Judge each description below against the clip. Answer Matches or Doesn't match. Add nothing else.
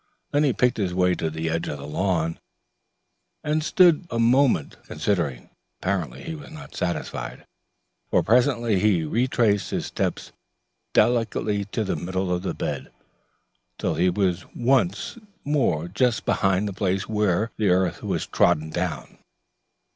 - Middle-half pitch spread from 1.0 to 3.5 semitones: Doesn't match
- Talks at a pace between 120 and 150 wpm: Matches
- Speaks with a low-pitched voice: Matches